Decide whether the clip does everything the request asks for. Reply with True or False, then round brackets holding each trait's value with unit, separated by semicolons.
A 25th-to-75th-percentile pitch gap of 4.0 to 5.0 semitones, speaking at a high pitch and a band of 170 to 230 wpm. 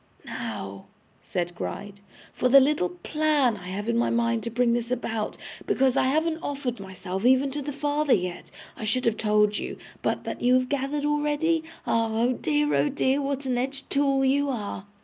True (4.7 semitones; 255 Hz; 190 wpm)